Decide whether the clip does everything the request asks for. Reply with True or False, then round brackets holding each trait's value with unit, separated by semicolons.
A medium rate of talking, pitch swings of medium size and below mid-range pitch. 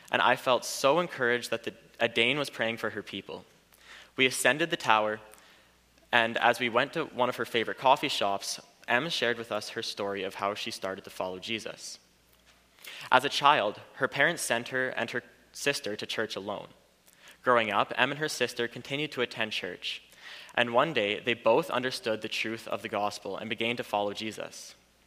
True (195 wpm; 3.0 semitones; 115 Hz)